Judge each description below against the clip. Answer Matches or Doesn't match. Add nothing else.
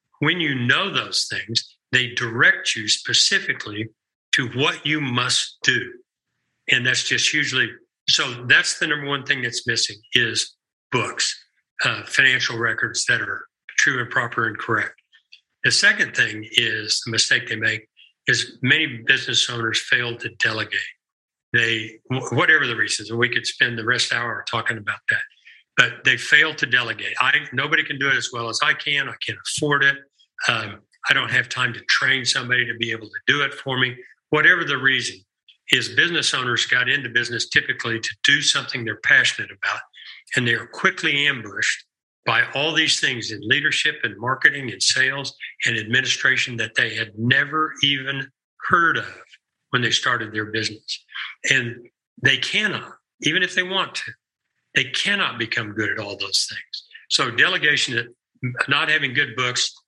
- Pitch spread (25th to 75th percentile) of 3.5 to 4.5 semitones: Matches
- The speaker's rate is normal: Matches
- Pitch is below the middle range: Matches